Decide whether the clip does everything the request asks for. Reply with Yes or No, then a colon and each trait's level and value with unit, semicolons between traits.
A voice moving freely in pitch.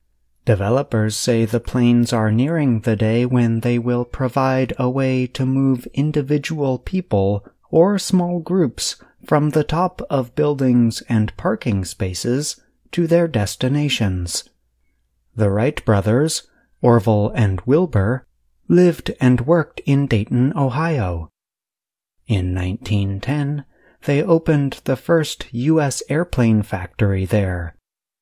Yes: wide, 5.7 semitones